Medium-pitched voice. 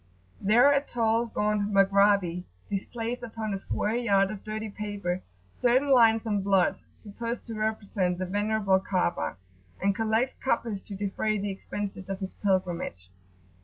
No: high, 205 Hz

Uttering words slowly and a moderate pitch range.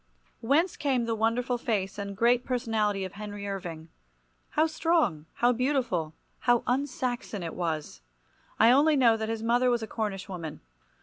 No: average, 165 wpm; average, 4.2 semitones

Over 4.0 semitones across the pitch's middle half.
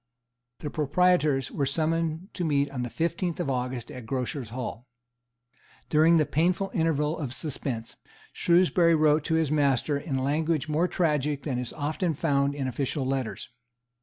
No: average, 3.5 semitones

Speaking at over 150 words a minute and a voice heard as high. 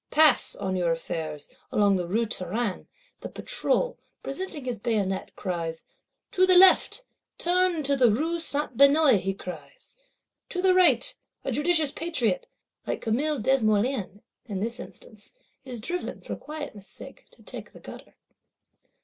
No: average, 145 wpm; very high, 250 Hz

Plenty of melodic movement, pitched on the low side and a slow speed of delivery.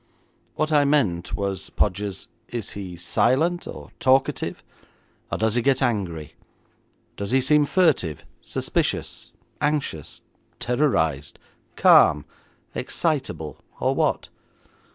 Yes: wide, 8.2 semitones; low, 120 Hz; slow, 105 wpm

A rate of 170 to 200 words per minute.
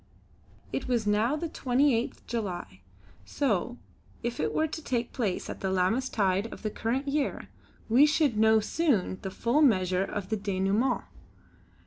No: average, 155 wpm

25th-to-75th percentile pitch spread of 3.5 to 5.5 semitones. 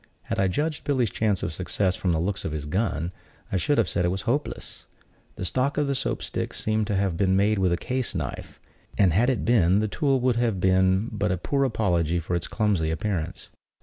Yes: average, 4.7 semitones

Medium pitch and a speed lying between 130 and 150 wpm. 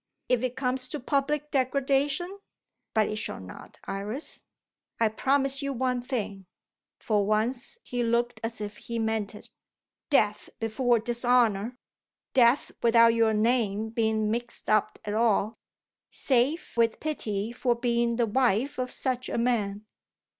No: high, 235 Hz; average, 140 wpm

